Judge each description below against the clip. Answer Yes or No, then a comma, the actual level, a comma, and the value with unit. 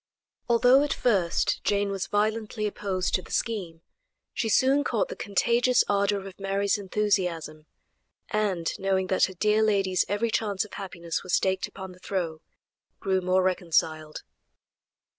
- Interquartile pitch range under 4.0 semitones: Yes, narrow, 2.6 semitones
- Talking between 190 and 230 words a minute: No, average, 145 wpm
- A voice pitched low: No, high, 195 Hz